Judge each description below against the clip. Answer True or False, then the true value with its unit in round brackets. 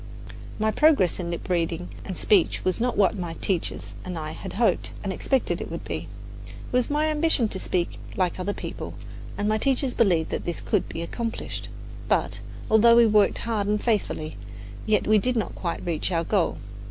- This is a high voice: True (205 Hz)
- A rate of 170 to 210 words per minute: True (190 wpm)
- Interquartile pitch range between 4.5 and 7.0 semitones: True (4.9 semitones)